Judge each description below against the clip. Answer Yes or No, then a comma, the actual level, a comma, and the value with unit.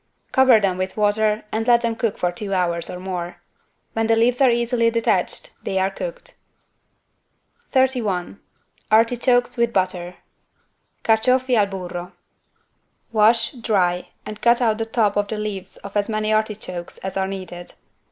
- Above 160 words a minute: No, average, 150 wpm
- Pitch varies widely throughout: No, average, 3.6 semitones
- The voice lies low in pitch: No, high, 215 Hz